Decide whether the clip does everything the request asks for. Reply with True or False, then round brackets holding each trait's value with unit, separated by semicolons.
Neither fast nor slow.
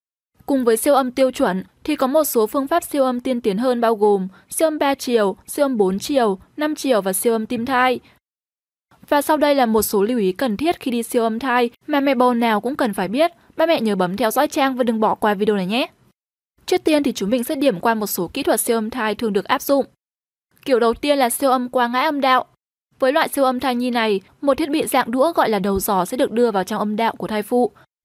False (270 wpm)